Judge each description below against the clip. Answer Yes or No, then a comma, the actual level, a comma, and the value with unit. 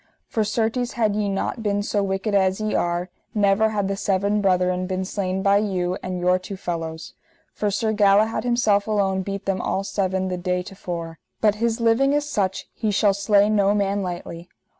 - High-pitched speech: Yes, high, 200 Hz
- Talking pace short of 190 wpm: No, average, 195 wpm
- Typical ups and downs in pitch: No, narrow, 2.2 semitones